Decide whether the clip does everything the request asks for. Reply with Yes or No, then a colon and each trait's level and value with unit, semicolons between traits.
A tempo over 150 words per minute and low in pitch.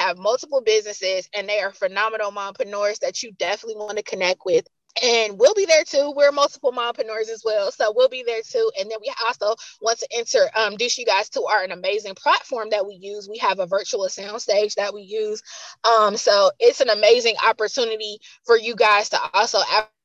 No: fast, 205 wpm; high, 220 Hz